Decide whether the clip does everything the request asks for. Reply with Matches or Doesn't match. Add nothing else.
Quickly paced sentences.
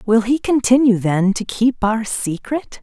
Doesn't match